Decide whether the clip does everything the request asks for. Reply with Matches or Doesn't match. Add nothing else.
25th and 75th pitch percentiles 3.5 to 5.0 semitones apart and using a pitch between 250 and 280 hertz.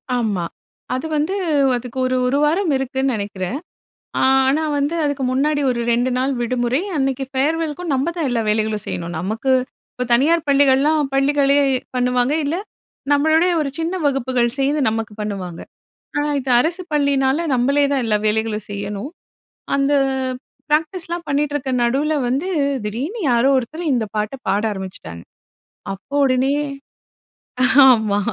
Matches